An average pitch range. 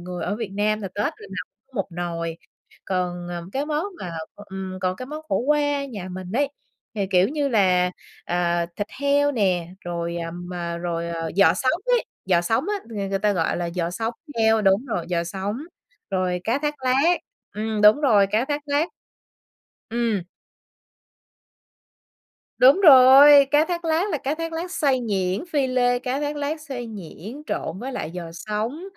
No: wide, 7.6 semitones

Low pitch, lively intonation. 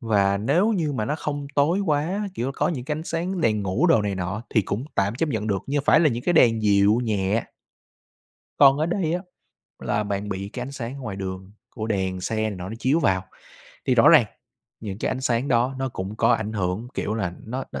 Yes: low, 115 Hz; wide, 6.1 semitones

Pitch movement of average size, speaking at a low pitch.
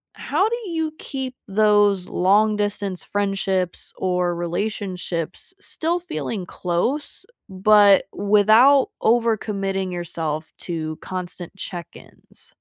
No: average, 3.5 semitones; high, 200 Hz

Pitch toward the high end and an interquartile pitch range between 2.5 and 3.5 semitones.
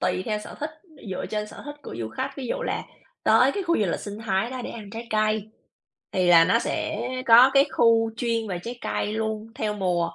Yes: high, 220 Hz; average, 3.1 semitones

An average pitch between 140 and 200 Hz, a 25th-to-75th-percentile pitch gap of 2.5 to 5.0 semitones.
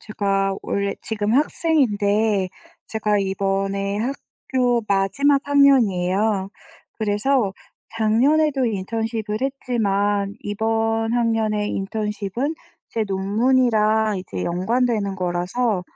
No: high, 215 Hz; average, 3.3 semitones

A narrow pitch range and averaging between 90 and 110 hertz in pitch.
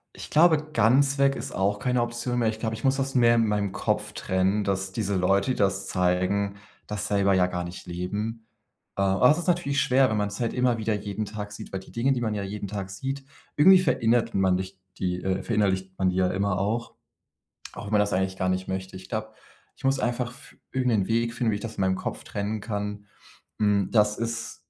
No: average, 3.5 semitones; low, 105 Hz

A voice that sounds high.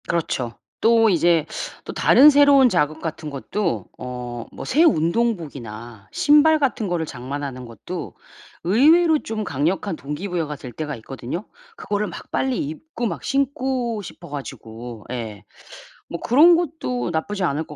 No: medium, 175 Hz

